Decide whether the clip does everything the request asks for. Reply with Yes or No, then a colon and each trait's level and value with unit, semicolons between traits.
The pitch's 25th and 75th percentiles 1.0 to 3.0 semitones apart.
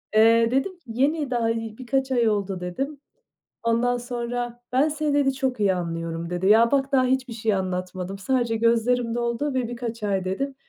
No: average, 3.9 semitones